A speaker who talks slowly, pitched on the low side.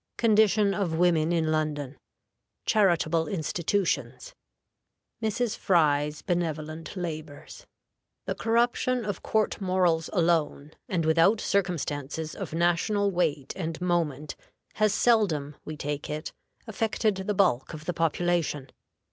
No: slow, 115 wpm; medium, 170 Hz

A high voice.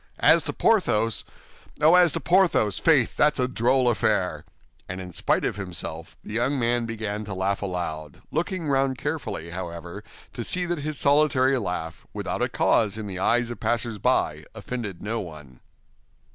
No: low, 115 Hz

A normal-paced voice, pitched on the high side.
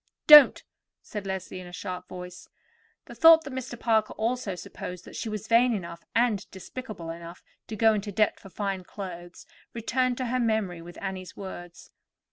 Yes: average, 175 wpm; high, 200 Hz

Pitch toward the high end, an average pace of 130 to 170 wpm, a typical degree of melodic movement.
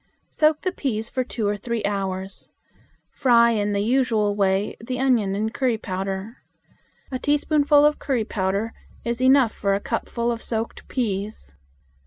Yes: high, 225 Hz; average, 155 wpm; average, 4.0 semitones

